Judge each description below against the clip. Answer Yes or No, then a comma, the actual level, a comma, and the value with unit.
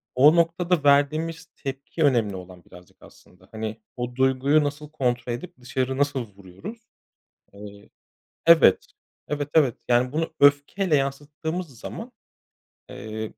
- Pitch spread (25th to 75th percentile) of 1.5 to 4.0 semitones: No, average, 4.9 semitones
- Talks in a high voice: No, low, 135 Hz